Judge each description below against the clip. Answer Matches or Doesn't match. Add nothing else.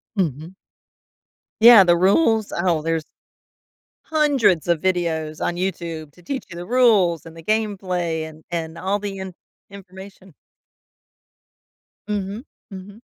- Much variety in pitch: Doesn't match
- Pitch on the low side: Doesn't match